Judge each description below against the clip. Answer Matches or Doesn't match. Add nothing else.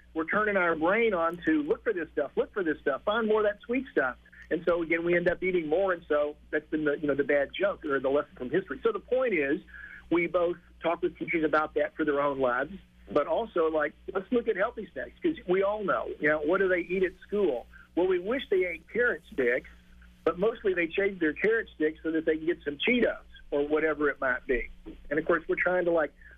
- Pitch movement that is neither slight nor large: Matches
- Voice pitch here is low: Doesn't match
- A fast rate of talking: Matches